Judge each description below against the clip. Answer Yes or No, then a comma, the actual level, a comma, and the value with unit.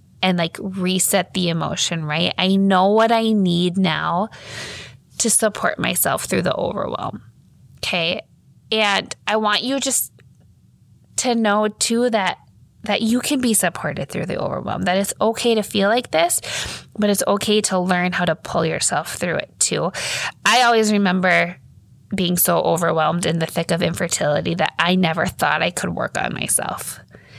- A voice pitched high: Yes, high, 195 Hz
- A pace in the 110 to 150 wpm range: No, average, 165 wpm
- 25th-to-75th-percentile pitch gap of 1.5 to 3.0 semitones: No, average, 3.9 semitones